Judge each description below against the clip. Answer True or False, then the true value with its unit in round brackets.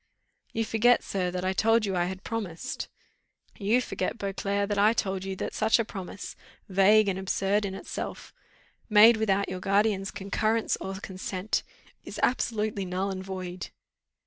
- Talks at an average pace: True (160 wpm)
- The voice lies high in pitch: True (200 Hz)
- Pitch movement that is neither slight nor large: False (2.3 semitones)